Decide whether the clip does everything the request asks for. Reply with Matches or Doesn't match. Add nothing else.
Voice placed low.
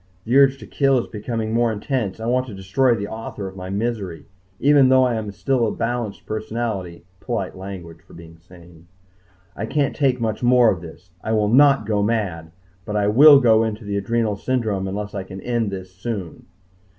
Matches